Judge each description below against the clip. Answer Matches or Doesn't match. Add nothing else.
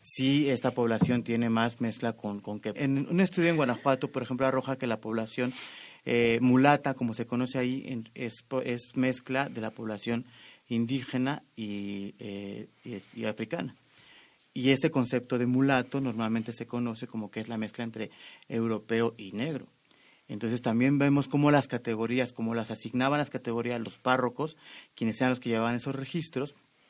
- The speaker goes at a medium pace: Matches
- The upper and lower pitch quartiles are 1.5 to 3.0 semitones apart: Matches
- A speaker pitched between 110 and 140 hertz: Matches